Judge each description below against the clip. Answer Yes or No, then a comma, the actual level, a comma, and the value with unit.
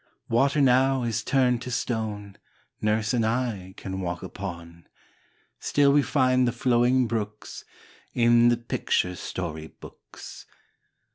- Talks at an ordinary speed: No, slow, 125 wpm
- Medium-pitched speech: No, low, 115 Hz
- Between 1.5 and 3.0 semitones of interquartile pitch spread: No, average, 3.7 semitones